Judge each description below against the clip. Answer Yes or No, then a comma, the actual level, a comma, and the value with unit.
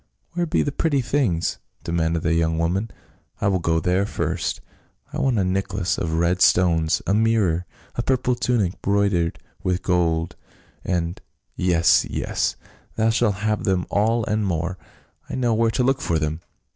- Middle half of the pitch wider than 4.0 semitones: Yes, average, 5.0 semitones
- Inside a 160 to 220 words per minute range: Yes, average, 190 wpm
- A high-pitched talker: No, very low, 95 Hz